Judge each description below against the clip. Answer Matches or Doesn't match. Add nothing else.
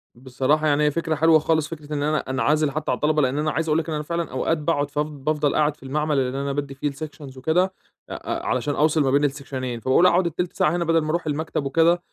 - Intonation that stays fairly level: Matches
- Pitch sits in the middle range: Matches